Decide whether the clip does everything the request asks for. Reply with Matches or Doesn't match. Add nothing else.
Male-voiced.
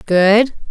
Doesn't match